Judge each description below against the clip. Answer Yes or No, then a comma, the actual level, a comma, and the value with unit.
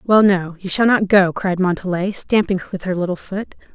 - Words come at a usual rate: Yes, average, 190 wpm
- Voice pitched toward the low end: No, high, 190 Hz